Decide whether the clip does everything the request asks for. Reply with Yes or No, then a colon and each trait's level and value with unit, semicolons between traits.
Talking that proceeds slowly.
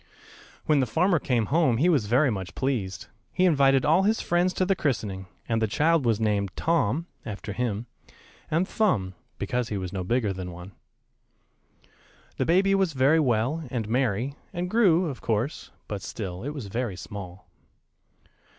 No: average, 170 wpm